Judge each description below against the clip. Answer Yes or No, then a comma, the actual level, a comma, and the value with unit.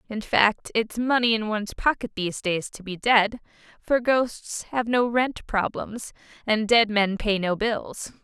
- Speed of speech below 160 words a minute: No, average, 175 wpm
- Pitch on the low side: No, high, 220 Hz